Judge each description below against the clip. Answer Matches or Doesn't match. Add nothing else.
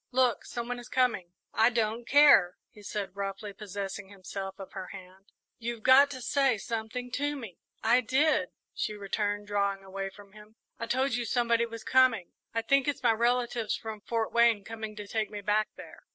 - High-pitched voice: Matches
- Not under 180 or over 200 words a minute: Matches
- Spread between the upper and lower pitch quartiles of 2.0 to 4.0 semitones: Matches